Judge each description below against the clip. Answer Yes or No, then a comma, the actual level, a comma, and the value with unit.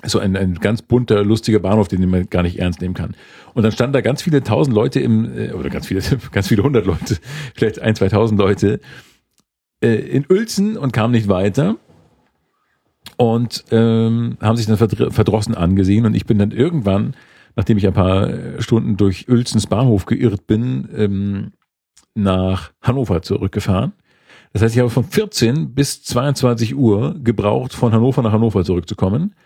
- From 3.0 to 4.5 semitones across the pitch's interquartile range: Yes, average, 3.5 semitones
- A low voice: Yes, low, 110 Hz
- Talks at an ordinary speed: Yes, average, 165 wpm